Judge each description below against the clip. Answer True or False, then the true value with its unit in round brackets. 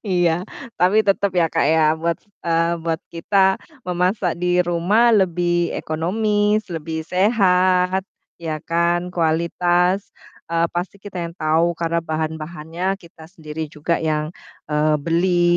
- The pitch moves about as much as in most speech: False (2.2 semitones)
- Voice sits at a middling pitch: True (175 Hz)